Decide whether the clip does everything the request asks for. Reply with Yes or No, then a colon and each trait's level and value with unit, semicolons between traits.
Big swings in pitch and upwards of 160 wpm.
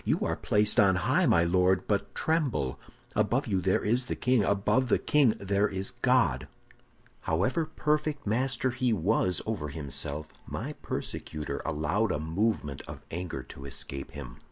No: wide, 7.6 semitones; average, 155 wpm